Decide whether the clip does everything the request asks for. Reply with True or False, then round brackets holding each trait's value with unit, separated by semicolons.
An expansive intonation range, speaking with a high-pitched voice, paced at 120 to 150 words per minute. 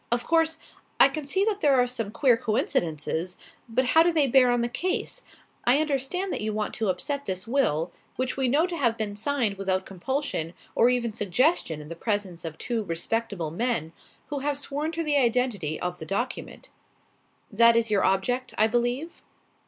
False (6.1 semitones; 235 Hz; 190 wpm)